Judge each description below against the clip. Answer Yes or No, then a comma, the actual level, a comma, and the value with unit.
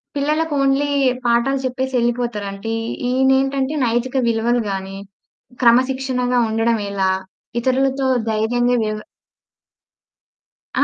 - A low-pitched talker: No, high, 245 Hz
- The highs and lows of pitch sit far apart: No, average, 2.8 semitones